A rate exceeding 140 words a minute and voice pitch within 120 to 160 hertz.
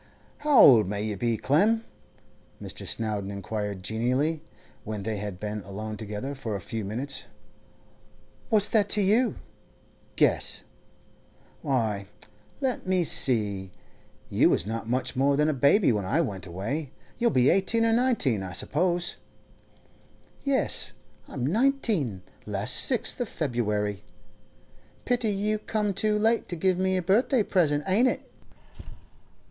No: slow, 135 wpm; medium, 140 Hz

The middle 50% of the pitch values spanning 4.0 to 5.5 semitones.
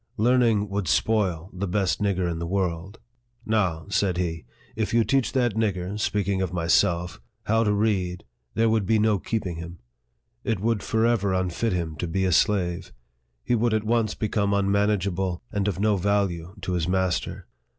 No: average, 3.4 semitones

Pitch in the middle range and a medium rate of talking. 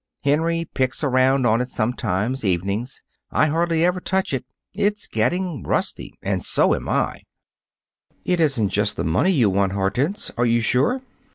No: low, 130 Hz; average, 160 wpm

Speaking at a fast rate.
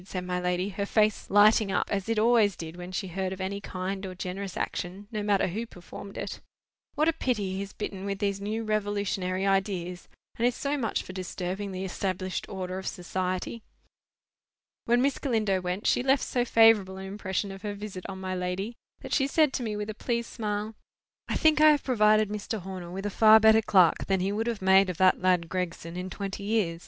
Yes: fast, 215 wpm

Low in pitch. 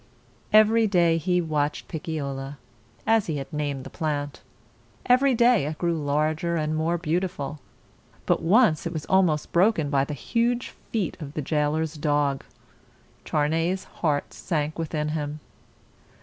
No: medium, 155 Hz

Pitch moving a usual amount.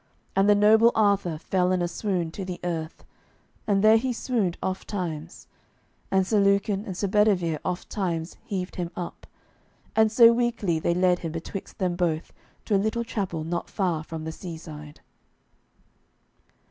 Yes: average, 3.5 semitones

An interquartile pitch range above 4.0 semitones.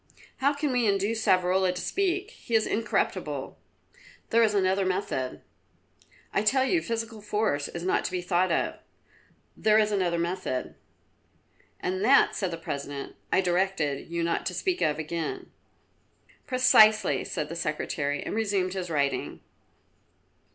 Yes: average, 4.5 semitones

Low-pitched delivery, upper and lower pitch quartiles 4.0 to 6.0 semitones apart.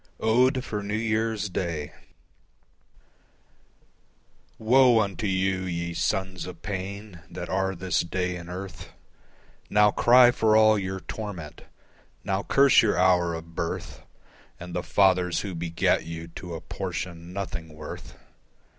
No: very low, 95 Hz; average, 3.3 semitones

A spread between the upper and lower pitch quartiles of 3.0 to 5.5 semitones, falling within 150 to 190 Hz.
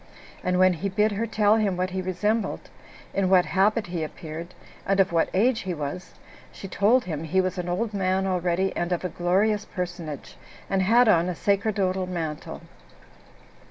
No: narrow, 2.4 semitones; medium, 185 Hz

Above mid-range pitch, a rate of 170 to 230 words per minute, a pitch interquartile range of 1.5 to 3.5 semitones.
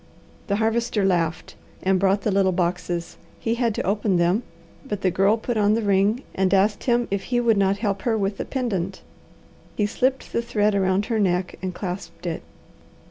Yes: high, 200 Hz; average, 190 wpm; average, 3.0 semitones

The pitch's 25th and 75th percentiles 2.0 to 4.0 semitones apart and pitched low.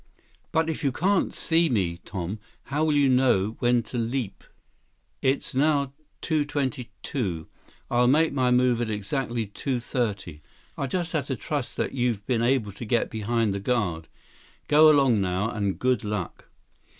No: average, 4.9 semitones; low, 125 Hz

